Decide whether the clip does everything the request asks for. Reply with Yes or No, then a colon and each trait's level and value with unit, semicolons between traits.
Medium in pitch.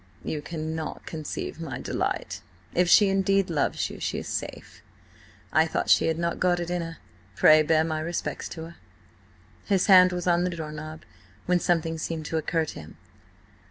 Yes: medium, 165 Hz